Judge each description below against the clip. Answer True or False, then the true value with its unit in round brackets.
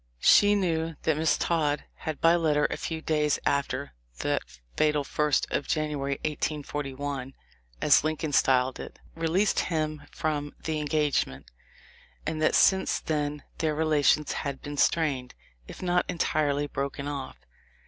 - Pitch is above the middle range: False (150 Hz)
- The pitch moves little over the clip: True (1.9 semitones)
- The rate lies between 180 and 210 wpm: False (140 wpm)